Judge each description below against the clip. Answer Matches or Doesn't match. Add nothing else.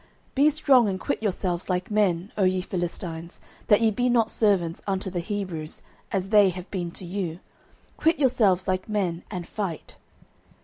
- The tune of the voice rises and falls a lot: Doesn't match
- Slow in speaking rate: Doesn't match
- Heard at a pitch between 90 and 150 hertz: Doesn't match